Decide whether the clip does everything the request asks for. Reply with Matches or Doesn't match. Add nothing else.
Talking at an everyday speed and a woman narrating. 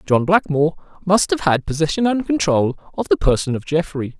Doesn't match